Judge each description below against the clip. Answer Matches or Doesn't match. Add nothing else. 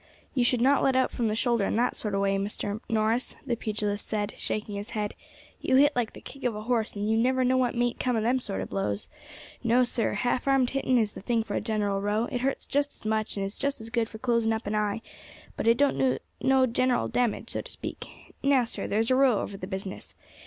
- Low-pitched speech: Doesn't match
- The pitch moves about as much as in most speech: Matches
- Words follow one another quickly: Matches